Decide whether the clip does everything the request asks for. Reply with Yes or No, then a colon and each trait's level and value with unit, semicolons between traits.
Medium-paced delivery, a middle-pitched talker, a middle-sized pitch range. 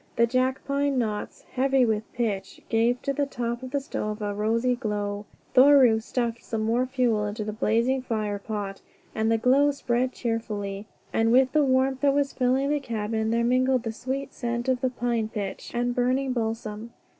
No: average, 180 wpm; high, 235 Hz; average, 3.0 semitones